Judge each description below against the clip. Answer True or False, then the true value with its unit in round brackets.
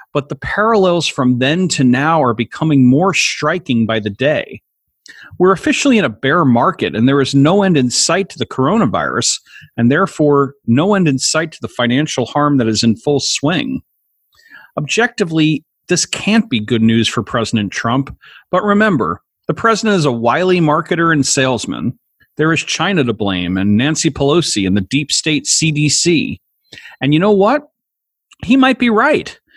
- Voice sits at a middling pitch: True (145 Hz)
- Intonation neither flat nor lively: False (6.2 semitones)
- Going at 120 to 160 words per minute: False (170 wpm)